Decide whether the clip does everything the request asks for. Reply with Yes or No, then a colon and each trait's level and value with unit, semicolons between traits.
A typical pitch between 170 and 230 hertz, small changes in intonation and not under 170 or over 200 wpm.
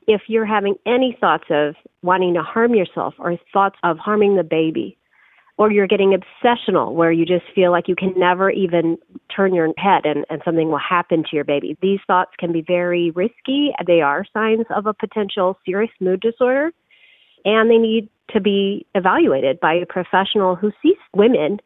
No: high, 190 Hz; average, 3.7 semitones; average, 185 wpm